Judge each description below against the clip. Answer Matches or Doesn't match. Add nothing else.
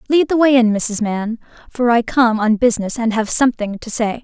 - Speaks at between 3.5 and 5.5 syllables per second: Matches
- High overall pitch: Matches